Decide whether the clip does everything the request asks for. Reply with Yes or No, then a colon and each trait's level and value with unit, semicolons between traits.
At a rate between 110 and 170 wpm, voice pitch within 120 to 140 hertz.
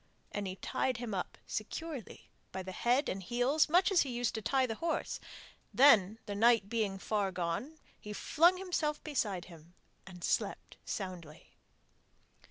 No: average, 160 wpm; high, 225 Hz